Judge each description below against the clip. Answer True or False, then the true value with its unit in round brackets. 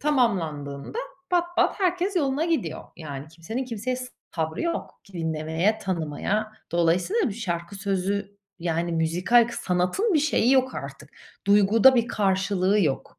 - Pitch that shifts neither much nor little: False (7.1 semitones)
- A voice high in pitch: True (200 Hz)